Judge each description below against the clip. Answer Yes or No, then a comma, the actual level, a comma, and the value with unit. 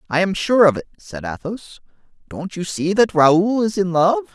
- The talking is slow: No, fast, 205 wpm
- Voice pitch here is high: No, medium, 180 Hz